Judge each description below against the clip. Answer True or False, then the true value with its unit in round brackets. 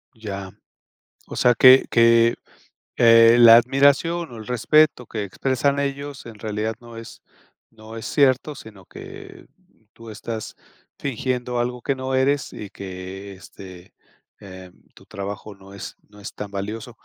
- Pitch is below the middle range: True (115 Hz)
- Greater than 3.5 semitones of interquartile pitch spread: True (4.2 semitones)